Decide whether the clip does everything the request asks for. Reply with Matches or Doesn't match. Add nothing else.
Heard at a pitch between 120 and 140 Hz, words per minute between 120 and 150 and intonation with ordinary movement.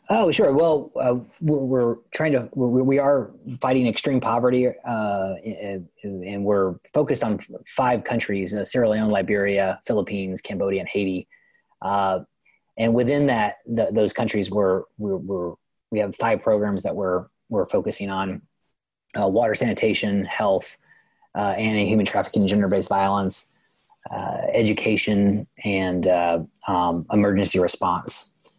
Doesn't match